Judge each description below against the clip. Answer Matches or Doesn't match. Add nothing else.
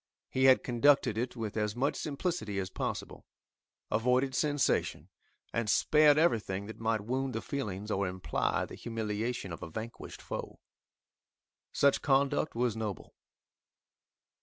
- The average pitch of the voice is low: Matches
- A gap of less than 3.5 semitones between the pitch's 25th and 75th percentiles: Doesn't match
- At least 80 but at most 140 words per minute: Matches